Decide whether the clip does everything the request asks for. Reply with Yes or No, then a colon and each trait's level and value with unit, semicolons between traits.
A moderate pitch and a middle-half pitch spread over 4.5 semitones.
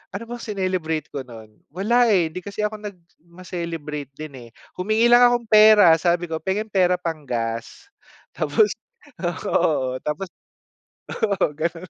Yes: medium, 180 Hz; average, 5.3 semitones